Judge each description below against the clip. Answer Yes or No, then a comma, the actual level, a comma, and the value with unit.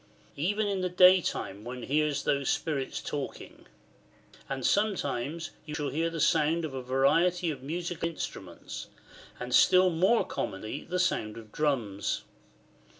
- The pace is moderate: Yes, average, 150 wpm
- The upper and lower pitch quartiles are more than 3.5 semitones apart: Yes, average, 5.2 semitones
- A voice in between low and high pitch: Yes, medium, 150 Hz